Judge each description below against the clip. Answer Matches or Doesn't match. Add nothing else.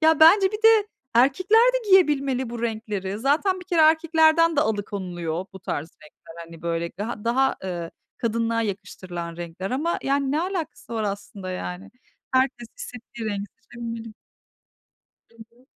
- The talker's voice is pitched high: Matches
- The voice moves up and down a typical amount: Doesn't match